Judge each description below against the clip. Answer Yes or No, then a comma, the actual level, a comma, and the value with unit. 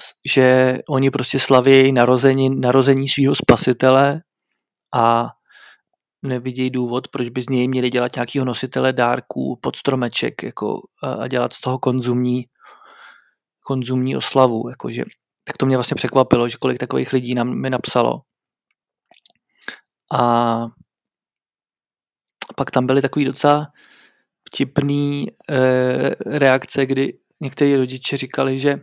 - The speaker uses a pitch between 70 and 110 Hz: No, low, 130 Hz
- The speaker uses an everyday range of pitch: No, narrow, 1.3 semitones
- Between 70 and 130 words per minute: Yes, average, 120 wpm